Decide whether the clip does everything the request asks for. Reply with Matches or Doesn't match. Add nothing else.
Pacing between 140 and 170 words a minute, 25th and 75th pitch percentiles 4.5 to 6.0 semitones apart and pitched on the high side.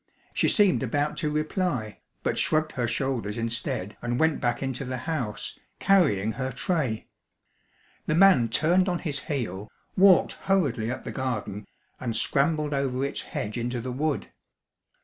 Doesn't match